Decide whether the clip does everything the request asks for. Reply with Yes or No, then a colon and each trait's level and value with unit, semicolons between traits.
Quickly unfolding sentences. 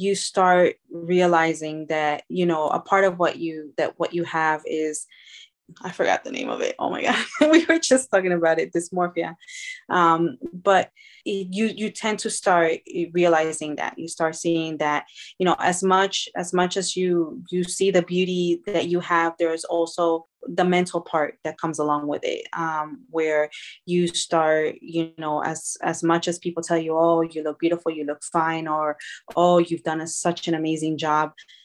No: average, 190 wpm